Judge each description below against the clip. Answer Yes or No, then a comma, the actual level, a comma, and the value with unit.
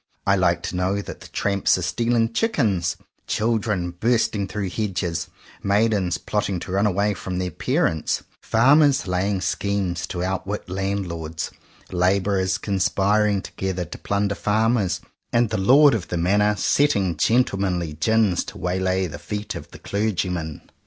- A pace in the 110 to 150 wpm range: Yes, average, 140 wpm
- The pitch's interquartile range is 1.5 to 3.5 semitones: Yes, average, 2.7 semitones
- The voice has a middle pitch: No, low, 100 Hz